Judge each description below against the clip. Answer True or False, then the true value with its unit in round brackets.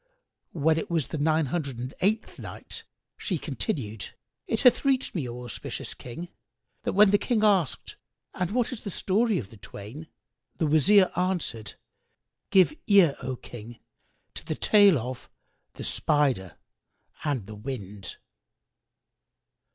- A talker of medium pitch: True (155 Hz)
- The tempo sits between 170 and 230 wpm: False (145 wpm)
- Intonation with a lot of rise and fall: True (7.9 semitones)